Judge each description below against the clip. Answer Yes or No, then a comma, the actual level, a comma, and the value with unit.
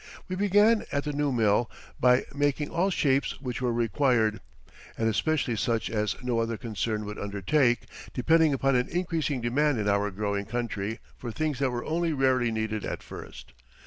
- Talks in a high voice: No, low, 125 Hz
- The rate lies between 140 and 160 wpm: No, average, 175 wpm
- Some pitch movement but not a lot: Yes, average, 4.9 semitones